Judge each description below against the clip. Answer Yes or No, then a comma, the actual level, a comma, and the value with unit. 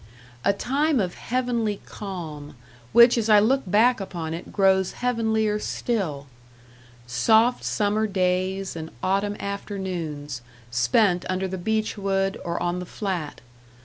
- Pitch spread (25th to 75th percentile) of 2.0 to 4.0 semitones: Yes, average, 3.7 semitones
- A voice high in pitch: Yes, high, 195 Hz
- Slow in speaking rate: Yes, slow, 130 wpm